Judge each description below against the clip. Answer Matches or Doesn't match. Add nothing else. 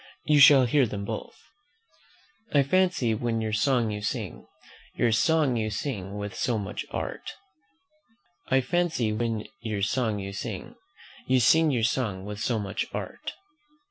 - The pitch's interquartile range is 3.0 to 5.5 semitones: Matches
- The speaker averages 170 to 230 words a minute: Doesn't match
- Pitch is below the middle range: Matches